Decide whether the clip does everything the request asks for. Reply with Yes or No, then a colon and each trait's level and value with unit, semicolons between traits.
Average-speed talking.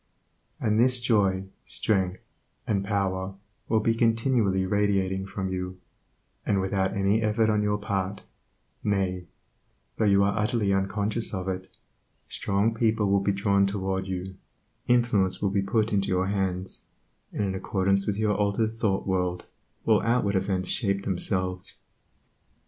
Yes: average, 145 wpm